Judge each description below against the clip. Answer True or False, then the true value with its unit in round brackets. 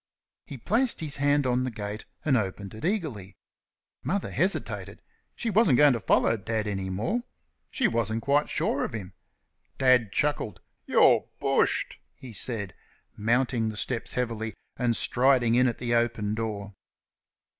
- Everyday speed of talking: True (150 wpm)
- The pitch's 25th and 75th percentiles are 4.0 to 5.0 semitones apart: True (4.4 semitones)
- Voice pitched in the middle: False (120 Hz)